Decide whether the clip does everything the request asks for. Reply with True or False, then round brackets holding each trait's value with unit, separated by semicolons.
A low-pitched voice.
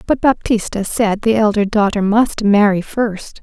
False (210 Hz)